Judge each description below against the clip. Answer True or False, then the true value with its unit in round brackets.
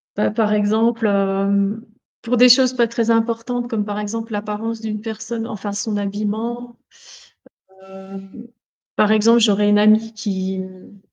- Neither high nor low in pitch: False (215 Hz)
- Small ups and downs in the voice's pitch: True (2.0 semitones)